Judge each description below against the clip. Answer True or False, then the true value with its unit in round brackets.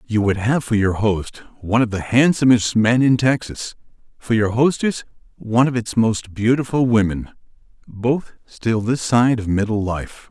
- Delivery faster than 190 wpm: False (165 wpm)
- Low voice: True (115 Hz)